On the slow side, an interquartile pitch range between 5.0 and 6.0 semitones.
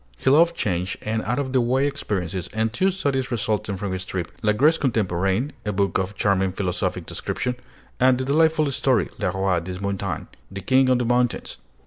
No: average, 190 wpm; wide, 5.5 semitones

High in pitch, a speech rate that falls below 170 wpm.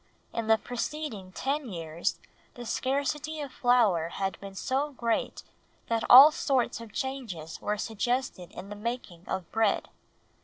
Yes: high, 230 Hz; average, 145 wpm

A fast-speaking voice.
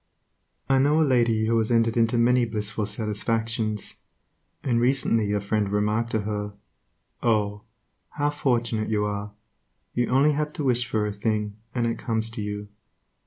No: average, 165 wpm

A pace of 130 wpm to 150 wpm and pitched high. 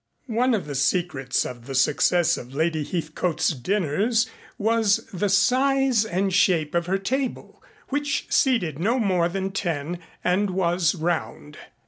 No: average, 140 wpm; medium, 180 Hz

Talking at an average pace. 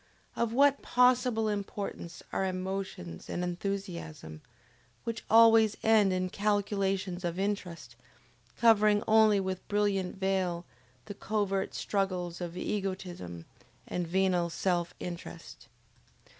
No: slow, 105 wpm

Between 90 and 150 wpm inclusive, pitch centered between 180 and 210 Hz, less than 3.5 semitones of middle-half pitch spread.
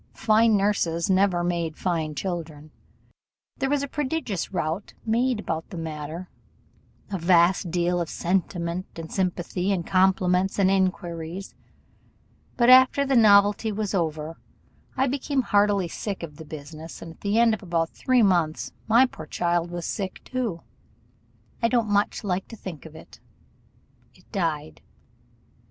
No: average, 145 wpm; medium, 185 Hz; average, 4.0 semitones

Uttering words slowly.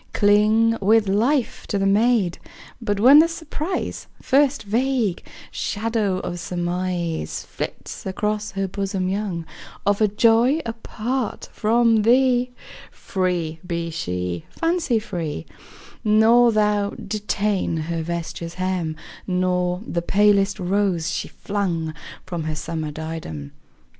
Yes: slow, 120 wpm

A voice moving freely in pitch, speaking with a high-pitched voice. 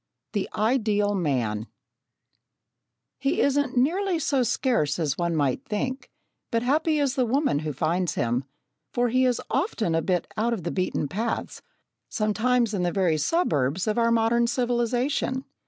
Yes: wide, 6.9 semitones; high, 225 Hz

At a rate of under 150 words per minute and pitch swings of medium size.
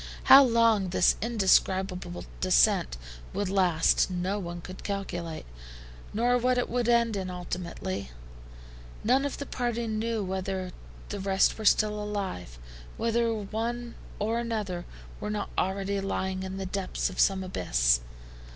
Yes: average, 140 wpm; average, 3.8 semitones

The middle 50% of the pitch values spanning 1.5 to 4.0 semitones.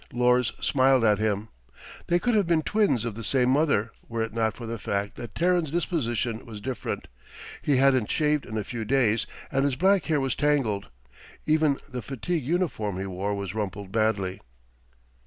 No: wide, 5.4 semitones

